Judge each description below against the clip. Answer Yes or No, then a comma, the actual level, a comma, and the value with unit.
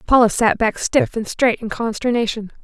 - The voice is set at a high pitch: Yes, high, 230 Hz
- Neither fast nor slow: Yes, average, 180 wpm